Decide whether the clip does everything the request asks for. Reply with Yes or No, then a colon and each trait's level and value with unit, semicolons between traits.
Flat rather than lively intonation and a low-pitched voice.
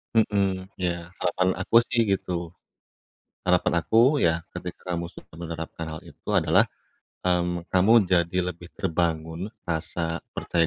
Yes: narrow, 1.8 semitones; very low, 90 Hz